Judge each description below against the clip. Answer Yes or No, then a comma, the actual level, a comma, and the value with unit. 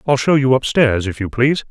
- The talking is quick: Yes, fast, 245 wpm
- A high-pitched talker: No, low, 125 Hz